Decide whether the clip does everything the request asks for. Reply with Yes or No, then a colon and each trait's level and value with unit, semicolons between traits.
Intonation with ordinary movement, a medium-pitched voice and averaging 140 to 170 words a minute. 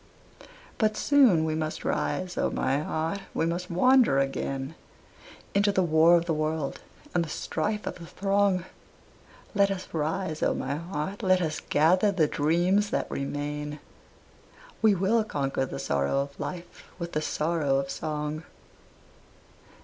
Yes: average, 4.3 semitones; medium, 165 Hz; average, 150 wpm